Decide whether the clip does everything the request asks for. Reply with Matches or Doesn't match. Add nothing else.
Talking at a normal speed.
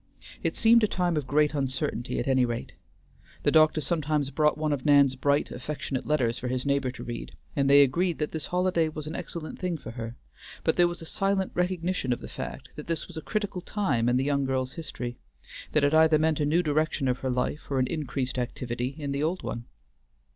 Doesn't match